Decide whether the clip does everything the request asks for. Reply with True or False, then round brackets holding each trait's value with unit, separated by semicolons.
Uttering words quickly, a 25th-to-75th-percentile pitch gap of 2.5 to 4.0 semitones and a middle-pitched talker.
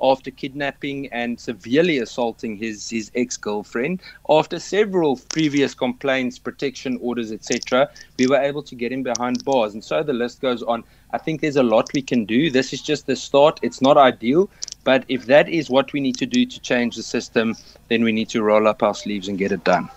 False (210 wpm; 2.9 semitones; 125 Hz)